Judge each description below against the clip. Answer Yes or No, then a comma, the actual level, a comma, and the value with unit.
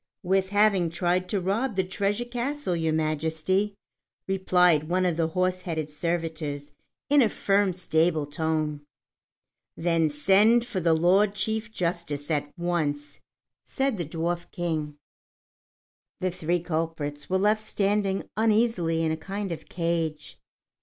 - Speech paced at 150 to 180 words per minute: No, slow, 135 wpm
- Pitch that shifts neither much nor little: Yes, average, 3.7 semitones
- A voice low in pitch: No, medium, 175 Hz